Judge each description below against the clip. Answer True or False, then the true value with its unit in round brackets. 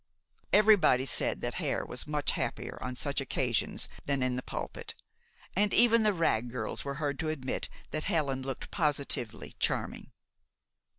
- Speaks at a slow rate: False (155 wpm)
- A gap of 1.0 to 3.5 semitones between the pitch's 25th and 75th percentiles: False (4.3 semitones)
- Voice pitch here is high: False (140 Hz)